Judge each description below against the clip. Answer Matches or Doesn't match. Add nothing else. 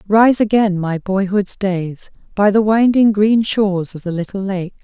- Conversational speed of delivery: Matches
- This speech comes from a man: Doesn't match